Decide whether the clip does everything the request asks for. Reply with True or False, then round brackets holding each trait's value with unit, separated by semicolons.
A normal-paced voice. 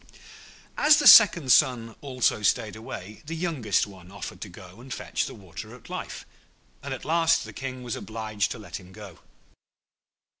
True (175 wpm)